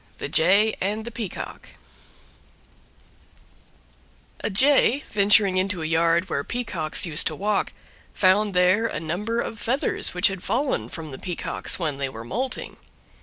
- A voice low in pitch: No, high, 190 Hz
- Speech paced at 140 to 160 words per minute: Yes, average, 145 wpm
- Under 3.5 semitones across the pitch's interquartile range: No, average, 4.9 semitones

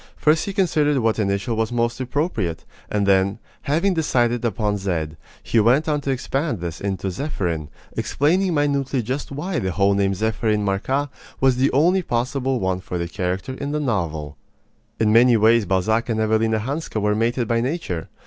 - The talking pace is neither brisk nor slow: Yes, average, 175 wpm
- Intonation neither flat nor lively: No, wide, 6.0 semitones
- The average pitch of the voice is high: No, low, 115 Hz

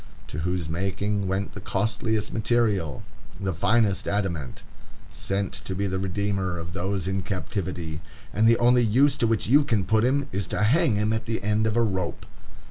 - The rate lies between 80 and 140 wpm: No, average, 185 wpm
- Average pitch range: Yes, average, 3.1 semitones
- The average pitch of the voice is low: Yes, low, 100 Hz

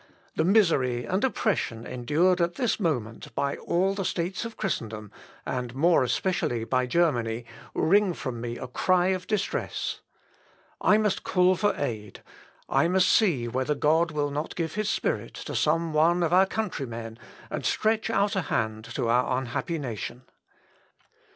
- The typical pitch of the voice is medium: Yes, medium, 160 Hz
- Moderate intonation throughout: No, wide, 7.2 semitones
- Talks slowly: No, average, 155 wpm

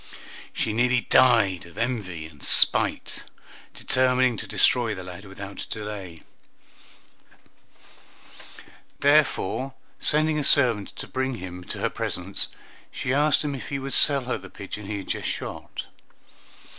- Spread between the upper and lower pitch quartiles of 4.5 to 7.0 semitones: Yes, average, 5.2 semitones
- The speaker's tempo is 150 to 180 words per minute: No, slow, 135 wpm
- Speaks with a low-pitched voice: Yes, low, 115 Hz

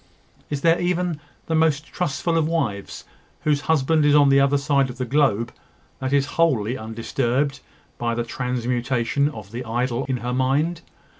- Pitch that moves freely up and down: No, average, 3.8 semitones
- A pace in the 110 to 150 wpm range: No, average, 165 wpm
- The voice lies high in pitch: No, low, 135 Hz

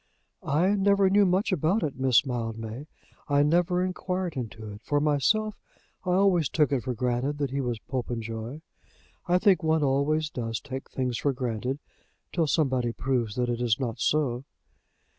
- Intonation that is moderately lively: No, wide, 5.9 semitones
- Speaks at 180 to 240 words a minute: No, average, 165 wpm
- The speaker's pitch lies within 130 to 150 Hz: Yes, medium, 140 Hz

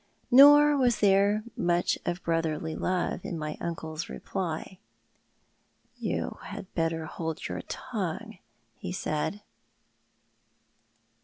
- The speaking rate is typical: No, slow, 105 wpm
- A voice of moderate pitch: Yes, medium, 175 Hz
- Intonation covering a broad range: No, average, 4.3 semitones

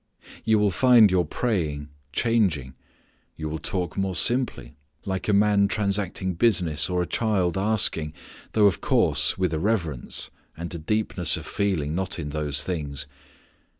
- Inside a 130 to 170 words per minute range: Yes, average, 150 wpm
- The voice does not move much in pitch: No, average, 5.0 semitones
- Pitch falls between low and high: No, very low, 90 Hz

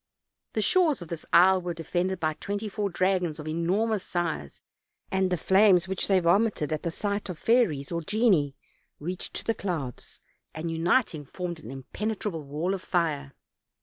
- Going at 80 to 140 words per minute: No, average, 170 wpm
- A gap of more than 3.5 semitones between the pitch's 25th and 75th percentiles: Yes, average, 3.9 semitones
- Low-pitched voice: No, medium, 180 Hz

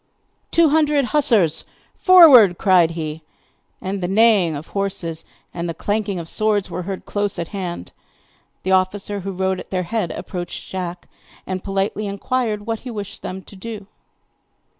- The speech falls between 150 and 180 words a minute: Yes, average, 160 wpm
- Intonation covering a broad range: No, average, 3.2 semitones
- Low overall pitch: No, high, 195 Hz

